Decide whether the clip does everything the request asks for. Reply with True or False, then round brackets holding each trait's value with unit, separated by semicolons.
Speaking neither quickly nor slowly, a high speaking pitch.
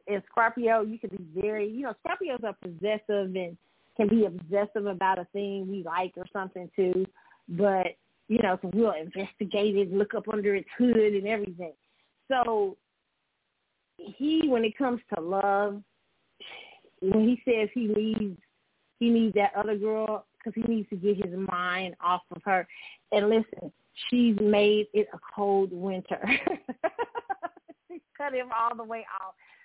True (155 wpm; 210 Hz)